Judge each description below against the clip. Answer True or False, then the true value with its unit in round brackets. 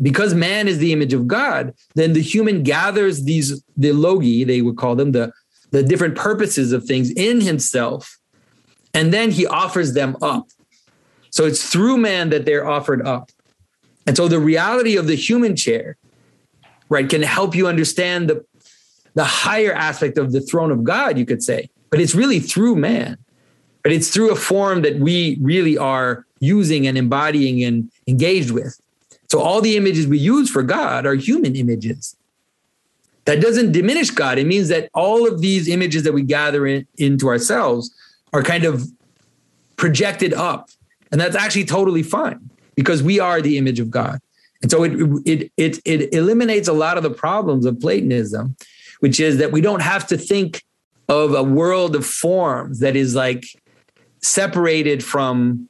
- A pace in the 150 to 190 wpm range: True (175 wpm)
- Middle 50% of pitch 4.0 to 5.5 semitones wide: True (5.2 semitones)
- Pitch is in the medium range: True (155 Hz)